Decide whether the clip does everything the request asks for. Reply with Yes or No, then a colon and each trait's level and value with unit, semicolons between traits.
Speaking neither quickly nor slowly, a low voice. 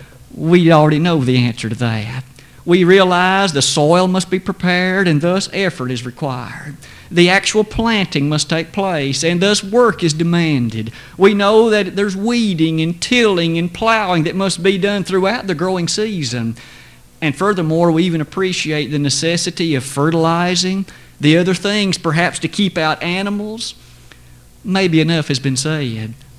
No: average, 155 wpm; medium, 170 Hz